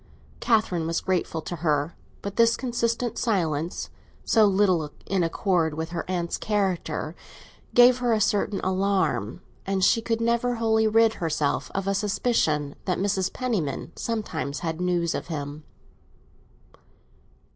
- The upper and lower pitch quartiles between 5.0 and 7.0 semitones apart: Yes, average, 5.3 semitones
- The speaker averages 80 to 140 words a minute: Yes, slow, 135 wpm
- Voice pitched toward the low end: No, high, 190 Hz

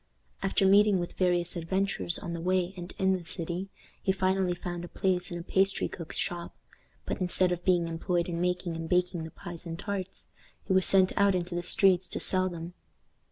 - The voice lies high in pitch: No, medium, 180 Hz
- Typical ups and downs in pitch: No, narrow, 1.6 semitones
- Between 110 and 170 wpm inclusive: No, fast, 205 wpm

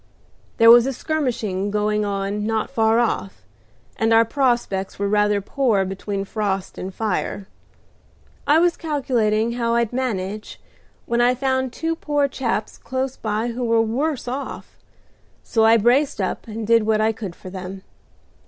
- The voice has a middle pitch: No, high, 225 Hz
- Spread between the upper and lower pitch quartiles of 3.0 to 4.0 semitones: Yes, average, 3.4 semitones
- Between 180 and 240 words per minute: No, average, 155 wpm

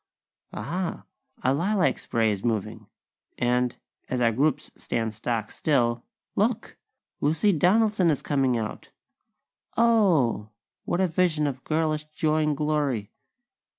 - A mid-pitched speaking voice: Yes, medium, 145 Hz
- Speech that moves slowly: Yes, slow, 120 wpm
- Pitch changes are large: Yes, wide, 5.7 semitones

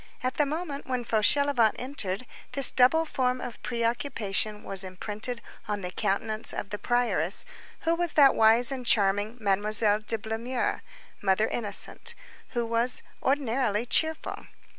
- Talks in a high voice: Yes, high, 230 Hz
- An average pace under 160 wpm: Yes, average, 140 wpm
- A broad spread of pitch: No, average, 3.8 semitones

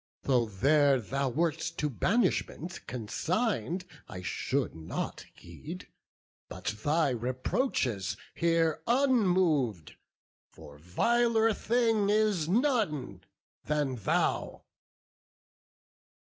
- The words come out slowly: Yes, slow, 85 wpm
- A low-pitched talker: No, medium, 150 Hz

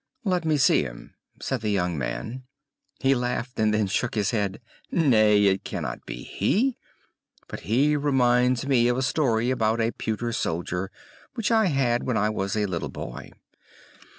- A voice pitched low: Yes, low, 120 Hz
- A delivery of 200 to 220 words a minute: No, average, 170 wpm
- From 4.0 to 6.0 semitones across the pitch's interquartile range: Yes, average, 4.3 semitones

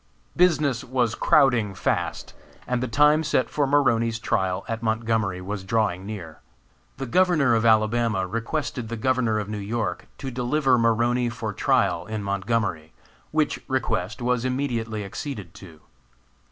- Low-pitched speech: Yes, low, 115 Hz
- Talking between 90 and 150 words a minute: Yes, average, 140 wpm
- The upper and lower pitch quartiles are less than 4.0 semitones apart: Yes, average, 3.6 semitones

